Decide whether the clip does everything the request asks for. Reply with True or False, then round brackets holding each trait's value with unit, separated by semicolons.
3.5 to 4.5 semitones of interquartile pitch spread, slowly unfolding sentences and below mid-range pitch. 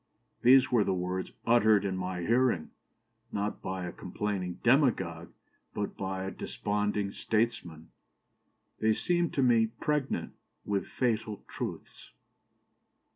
True (4.0 semitones; 120 wpm; 105 Hz)